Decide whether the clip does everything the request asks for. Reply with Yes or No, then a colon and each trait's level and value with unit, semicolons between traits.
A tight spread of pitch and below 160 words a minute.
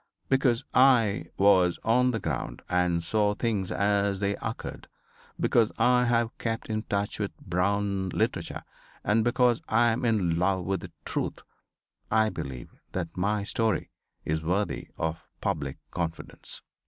No: average, 4.0 semitones; average, 140 wpm